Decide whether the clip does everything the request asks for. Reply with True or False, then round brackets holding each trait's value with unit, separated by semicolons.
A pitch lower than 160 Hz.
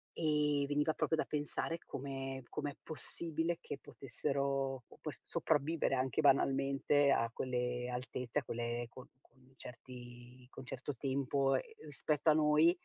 True (135 Hz)